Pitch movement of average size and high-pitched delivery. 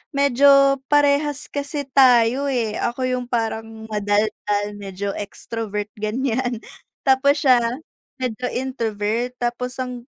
Yes: average, 3.5 semitones; high, 245 Hz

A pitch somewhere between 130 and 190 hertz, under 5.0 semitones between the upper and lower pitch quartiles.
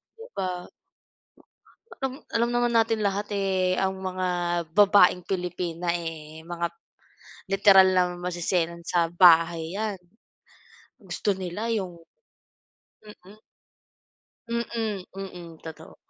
Yes: medium, 185 Hz; average, 2.9 semitones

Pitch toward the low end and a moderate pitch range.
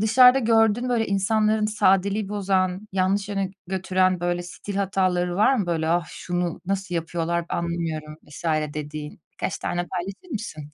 No: medium, 185 Hz; average, 3.1 semitones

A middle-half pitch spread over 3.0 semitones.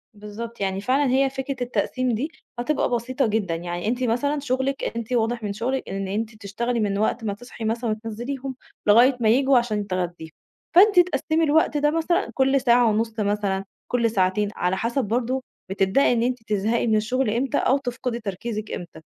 Yes: average, 3.9 semitones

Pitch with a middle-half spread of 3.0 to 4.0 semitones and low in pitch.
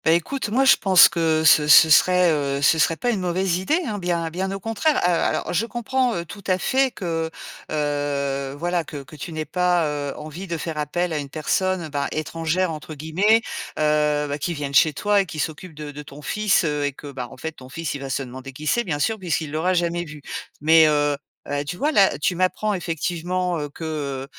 No: average, 3.7 semitones; medium, 160 Hz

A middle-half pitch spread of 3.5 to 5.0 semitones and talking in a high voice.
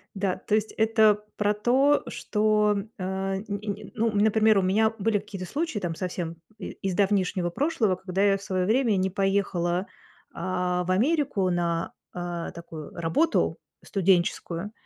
No: average, 2.8 semitones; high, 195 Hz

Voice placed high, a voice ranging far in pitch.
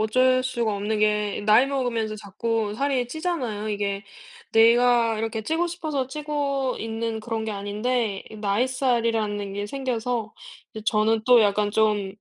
No: high, 225 Hz; average, 3.2 semitones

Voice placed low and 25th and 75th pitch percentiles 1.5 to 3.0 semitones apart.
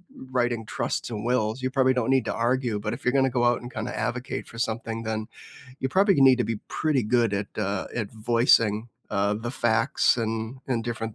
Yes: low, 120 Hz; narrow, 2.4 semitones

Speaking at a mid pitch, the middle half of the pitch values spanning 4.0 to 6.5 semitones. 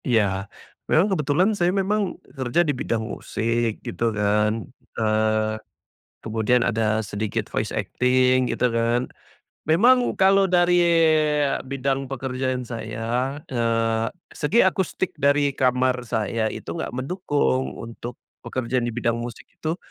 No: low, 125 Hz; average, 4.3 semitones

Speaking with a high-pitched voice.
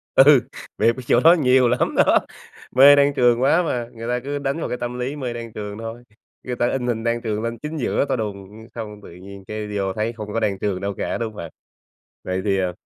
No: low, 115 Hz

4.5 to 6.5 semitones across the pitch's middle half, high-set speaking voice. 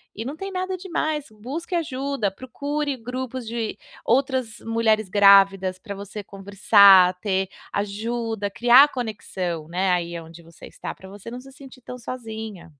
Yes: average, 4.9 semitones; high, 220 Hz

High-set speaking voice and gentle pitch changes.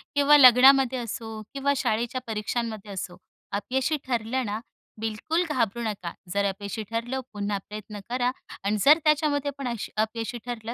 No: high, 235 Hz; average, 3.7 semitones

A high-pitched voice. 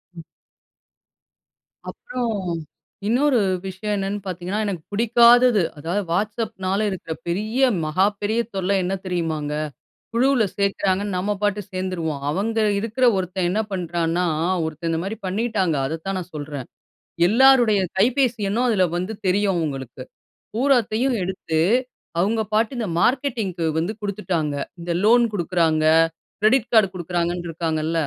Yes: high, 195 Hz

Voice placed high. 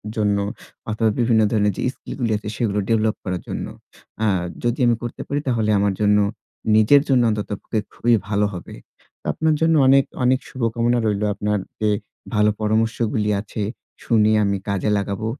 No: low, 110 Hz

